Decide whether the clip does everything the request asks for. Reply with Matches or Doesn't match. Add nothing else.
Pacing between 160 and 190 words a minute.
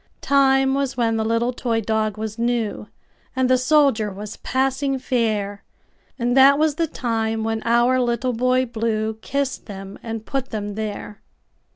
Doesn't match